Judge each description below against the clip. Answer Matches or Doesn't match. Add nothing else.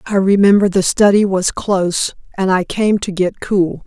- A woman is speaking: Matches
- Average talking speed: Matches